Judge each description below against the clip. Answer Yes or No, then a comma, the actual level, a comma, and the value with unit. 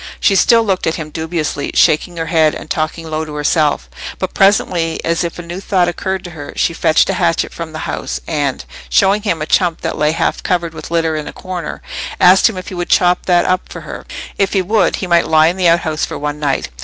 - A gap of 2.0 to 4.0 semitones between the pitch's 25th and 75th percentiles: Yes, average, 2.7 semitones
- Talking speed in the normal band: No, fast, 240 wpm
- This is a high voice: No, medium, 170 Hz